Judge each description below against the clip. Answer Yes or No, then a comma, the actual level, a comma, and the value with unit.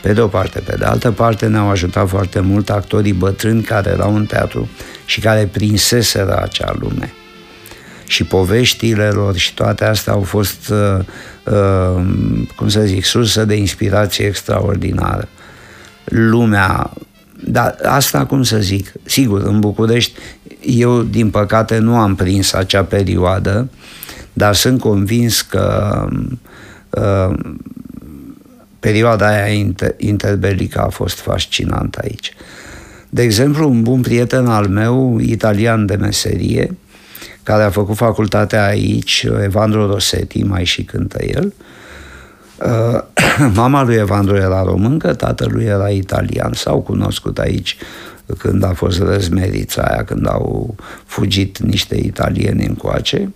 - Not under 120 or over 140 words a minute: Yes, average, 125 wpm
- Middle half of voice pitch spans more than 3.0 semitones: No, narrow, 2.5 semitones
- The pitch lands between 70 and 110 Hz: Yes, low, 105 Hz